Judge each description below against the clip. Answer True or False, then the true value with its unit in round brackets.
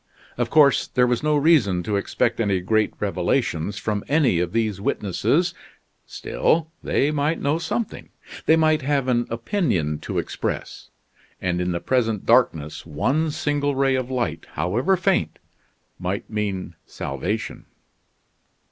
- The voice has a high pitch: False (120 Hz)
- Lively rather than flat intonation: True (7.1 semitones)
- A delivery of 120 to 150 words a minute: True (140 wpm)